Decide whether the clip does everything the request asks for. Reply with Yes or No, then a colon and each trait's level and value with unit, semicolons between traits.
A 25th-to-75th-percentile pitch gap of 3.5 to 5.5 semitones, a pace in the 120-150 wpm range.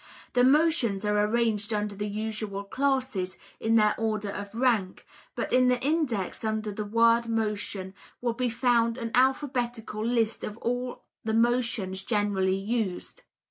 No: average, 2.9 semitones; average, 145 wpm